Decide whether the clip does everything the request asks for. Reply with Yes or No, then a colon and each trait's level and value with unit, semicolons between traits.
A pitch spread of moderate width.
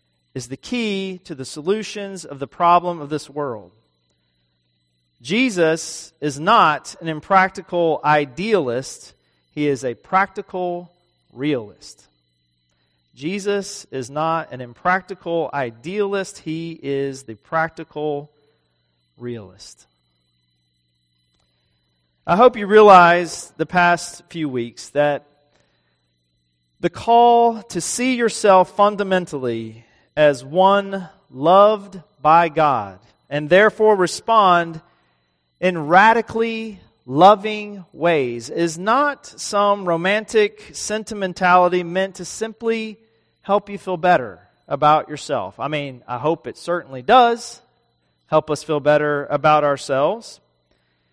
No: wide, 7.6 semitones